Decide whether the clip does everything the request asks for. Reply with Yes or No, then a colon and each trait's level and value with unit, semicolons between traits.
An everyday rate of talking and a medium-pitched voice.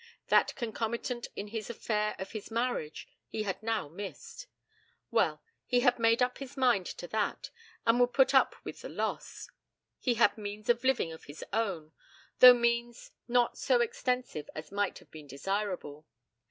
No: average, 165 wpm; high, 225 Hz